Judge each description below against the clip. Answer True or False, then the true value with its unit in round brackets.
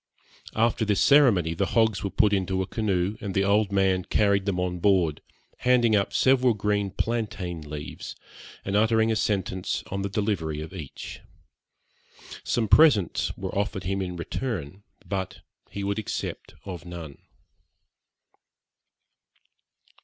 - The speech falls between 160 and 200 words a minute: False (140 wpm)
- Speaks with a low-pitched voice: True (100 Hz)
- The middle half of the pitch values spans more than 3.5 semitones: False (3.1 semitones)